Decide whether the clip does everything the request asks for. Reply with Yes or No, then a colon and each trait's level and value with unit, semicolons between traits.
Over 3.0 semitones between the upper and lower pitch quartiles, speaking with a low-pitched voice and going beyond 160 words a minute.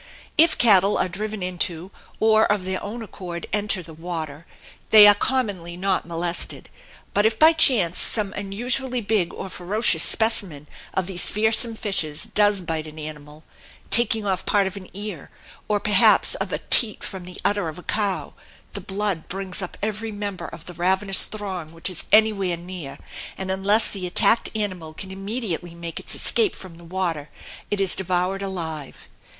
No: average, 3.4 semitones; high, 190 Hz; average, 170 wpm